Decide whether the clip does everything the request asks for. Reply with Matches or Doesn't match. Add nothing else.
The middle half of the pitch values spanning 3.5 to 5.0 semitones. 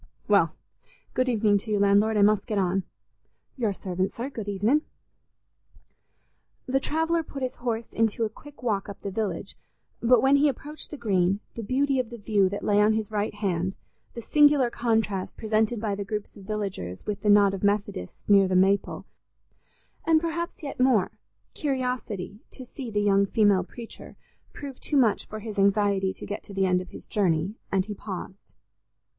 Matches